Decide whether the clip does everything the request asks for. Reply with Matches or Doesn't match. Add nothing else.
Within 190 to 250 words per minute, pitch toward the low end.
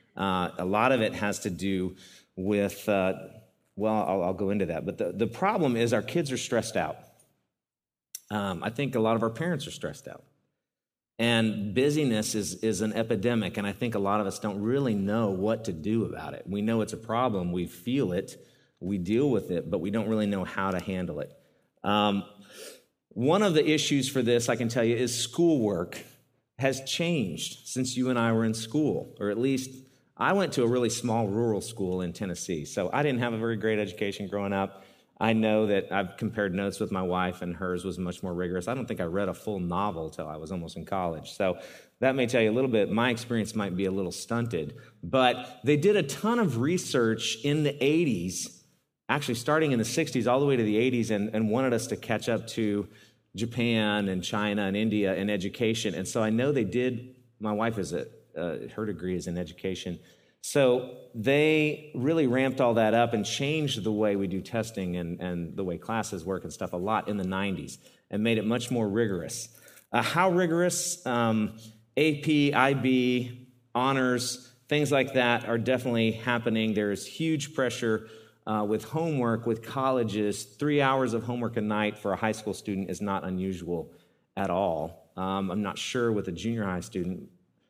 Matches